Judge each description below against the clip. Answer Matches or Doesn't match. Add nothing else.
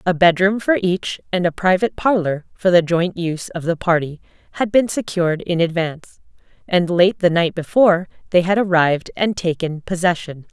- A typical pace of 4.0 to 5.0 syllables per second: Doesn't match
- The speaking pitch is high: Doesn't match